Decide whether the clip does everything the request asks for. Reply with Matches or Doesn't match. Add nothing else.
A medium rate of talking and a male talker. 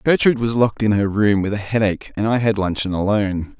Doesn't match